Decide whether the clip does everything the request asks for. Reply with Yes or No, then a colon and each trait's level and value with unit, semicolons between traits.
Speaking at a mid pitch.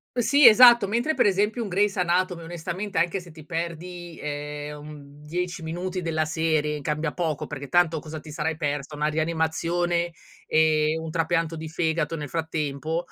Yes: medium, 165 Hz